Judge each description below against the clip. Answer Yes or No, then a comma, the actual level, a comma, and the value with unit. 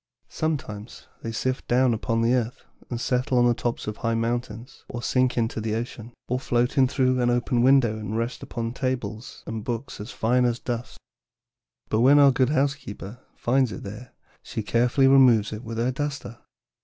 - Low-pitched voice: Yes, low, 120 Hz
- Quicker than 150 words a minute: Yes, average, 180 wpm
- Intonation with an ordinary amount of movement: No, narrow, 2.1 semitones